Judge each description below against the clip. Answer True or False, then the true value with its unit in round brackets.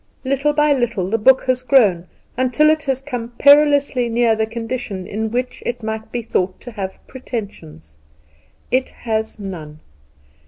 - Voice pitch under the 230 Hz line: False (235 Hz)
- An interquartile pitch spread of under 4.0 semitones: True (3.6 semitones)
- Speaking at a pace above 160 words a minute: False (155 wpm)